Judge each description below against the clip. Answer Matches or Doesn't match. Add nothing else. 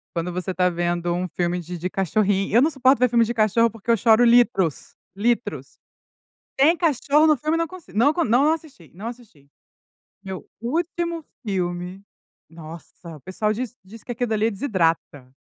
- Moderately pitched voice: Doesn't match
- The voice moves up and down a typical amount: Doesn't match